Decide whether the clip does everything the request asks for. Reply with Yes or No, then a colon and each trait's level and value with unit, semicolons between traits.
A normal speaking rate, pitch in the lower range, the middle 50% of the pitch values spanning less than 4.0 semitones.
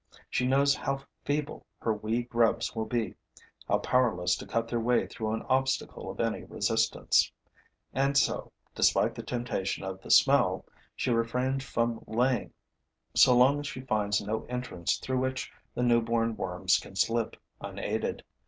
Yes: average, 155 wpm; low, 120 Hz; average, 2.8 semitones